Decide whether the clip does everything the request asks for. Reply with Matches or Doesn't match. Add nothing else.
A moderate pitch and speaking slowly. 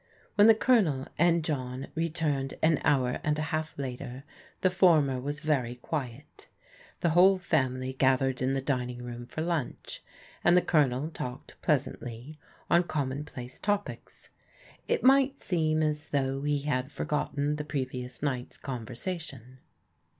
Doesn't match